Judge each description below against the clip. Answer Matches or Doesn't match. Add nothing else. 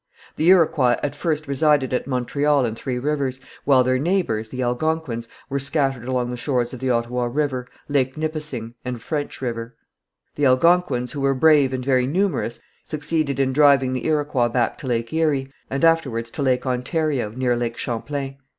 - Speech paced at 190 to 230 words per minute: Doesn't match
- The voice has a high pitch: Doesn't match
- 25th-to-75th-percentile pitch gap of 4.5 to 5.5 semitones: Doesn't match